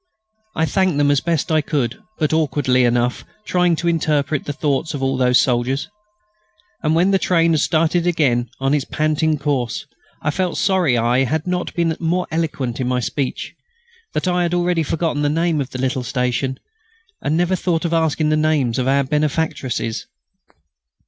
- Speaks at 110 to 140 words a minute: No, average, 180 wpm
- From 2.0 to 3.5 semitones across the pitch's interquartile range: No, average, 4.0 semitones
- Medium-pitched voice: Yes, medium, 150 Hz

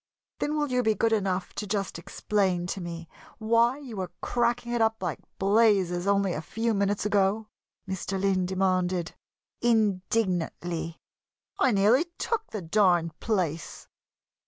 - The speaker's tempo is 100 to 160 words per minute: Yes, average, 140 wpm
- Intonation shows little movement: No, average, 3.7 semitones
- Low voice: No, high, 200 Hz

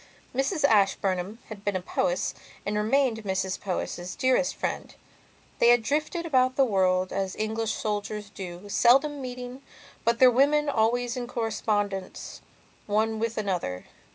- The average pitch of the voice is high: Yes, high, 220 Hz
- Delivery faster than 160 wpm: No, average, 140 wpm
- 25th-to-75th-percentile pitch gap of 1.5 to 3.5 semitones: No, average, 4.4 semitones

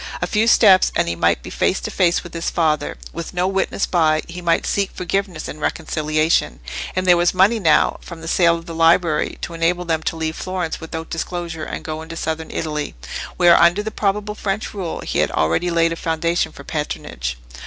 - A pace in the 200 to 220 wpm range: Yes, fast, 205 wpm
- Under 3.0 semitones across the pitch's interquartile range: Yes, narrow, 2.4 semitones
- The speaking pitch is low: No, medium, 170 Hz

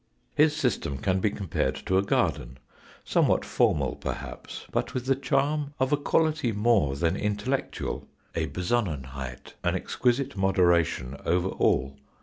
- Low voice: Yes, low, 100 Hz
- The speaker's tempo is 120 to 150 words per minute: Yes, slow, 135 wpm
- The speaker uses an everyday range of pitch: No, wide, 7.9 semitones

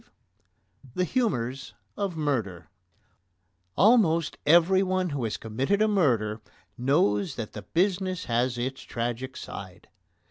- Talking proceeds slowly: Yes, slow, 115 wpm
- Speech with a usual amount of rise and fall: No, wide, 8.0 semitones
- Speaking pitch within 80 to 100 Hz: No, low, 135 Hz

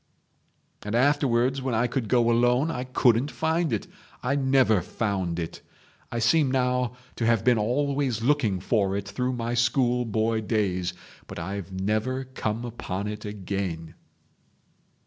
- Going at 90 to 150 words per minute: Yes, average, 145 wpm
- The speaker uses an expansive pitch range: No, average, 3.7 semitones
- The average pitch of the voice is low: Yes, low, 115 Hz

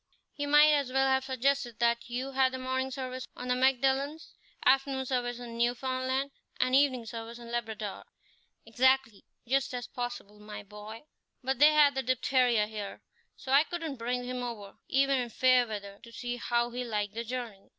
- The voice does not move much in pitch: Yes, narrow, 2.2 semitones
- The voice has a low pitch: No, very high, 250 Hz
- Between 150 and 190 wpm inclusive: Yes, average, 175 wpm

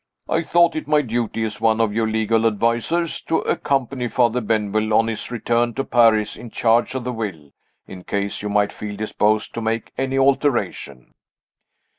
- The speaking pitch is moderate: No, low, 115 Hz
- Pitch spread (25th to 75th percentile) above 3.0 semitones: No, narrow, 2.6 semitones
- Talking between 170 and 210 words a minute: Yes, average, 175 wpm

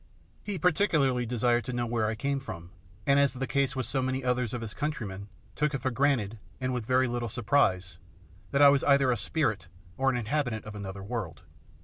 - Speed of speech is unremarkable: No, fast, 215 wpm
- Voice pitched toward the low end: Yes, low, 125 Hz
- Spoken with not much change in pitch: No, average, 4.1 semitones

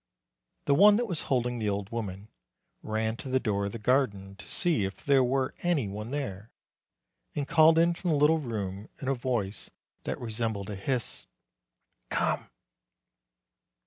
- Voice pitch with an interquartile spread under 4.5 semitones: No, wide, 5.5 semitones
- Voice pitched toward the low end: Yes, low, 120 Hz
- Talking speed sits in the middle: Yes, average, 165 wpm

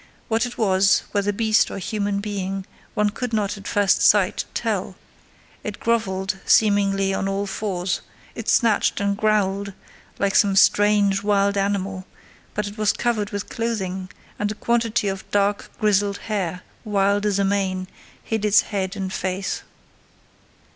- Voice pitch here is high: Yes, high, 200 Hz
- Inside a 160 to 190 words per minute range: No, average, 150 wpm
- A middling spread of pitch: No, narrow, 1.4 semitones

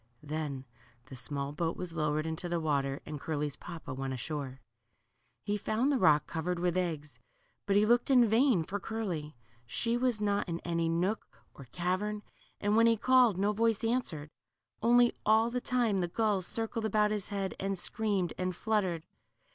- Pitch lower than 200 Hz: Yes, medium, 185 Hz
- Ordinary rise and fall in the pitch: No, wide, 5.7 semitones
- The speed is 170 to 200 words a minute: Yes, average, 175 wpm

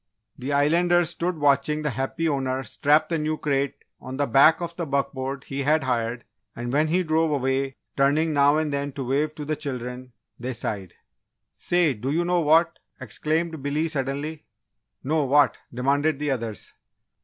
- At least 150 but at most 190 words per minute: Yes, average, 170 wpm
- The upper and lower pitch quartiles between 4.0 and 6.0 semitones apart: No, average, 2.8 semitones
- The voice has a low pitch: No, medium, 145 Hz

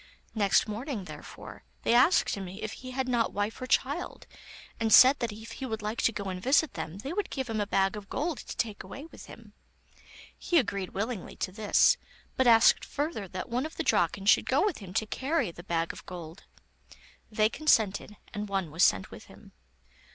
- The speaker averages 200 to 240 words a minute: Yes, fast, 205 wpm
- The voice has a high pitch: Yes, high, 220 Hz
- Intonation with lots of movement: No, average, 5.0 semitones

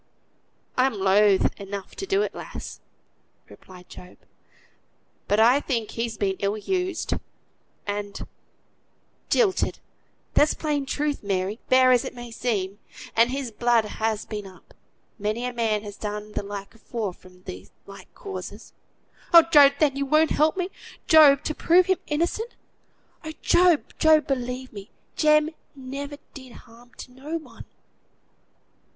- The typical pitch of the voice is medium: No, high, 245 Hz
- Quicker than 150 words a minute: No, average, 140 wpm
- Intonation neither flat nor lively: No, wide, 6.5 semitones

